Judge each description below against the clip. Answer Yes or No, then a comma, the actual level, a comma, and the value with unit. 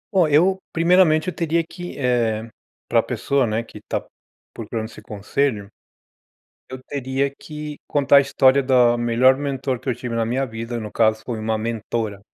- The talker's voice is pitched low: Yes, low, 130 Hz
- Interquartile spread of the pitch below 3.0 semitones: No, average, 3.8 semitones